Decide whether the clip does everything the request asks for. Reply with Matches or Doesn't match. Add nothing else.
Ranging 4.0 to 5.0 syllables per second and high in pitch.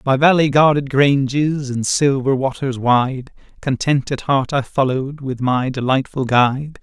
Doesn't match